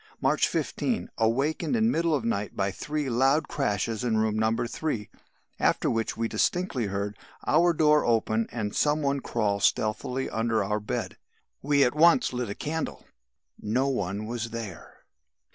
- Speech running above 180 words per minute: No, average, 160 wpm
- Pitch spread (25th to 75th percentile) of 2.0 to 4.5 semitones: No, average, 5.3 semitones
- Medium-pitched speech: No, low, 120 Hz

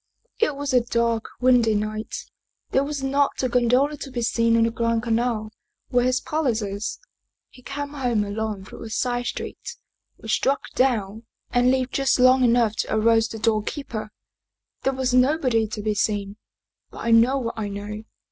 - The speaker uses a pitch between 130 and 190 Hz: No, high, 235 Hz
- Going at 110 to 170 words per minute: No, average, 180 wpm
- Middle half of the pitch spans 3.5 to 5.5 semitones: No, average, 2.9 semitones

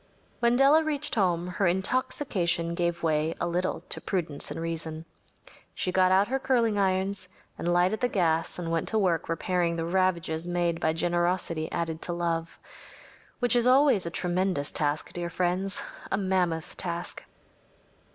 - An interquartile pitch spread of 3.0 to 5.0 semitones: No, narrow, 2.6 semitones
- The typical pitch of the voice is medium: Yes, medium, 175 Hz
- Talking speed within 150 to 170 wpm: Yes, average, 155 wpm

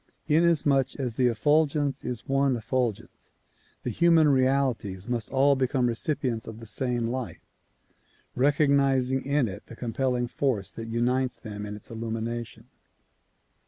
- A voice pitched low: Yes, low, 125 Hz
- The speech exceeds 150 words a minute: No, average, 140 wpm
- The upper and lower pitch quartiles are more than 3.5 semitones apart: No, average, 3.2 semitones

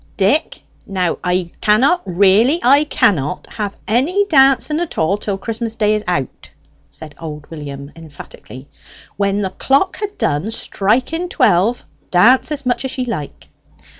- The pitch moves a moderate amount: No, wide, 6.9 semitones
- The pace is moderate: Yes, average, 145 wpm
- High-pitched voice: Yes, high, 210 Hz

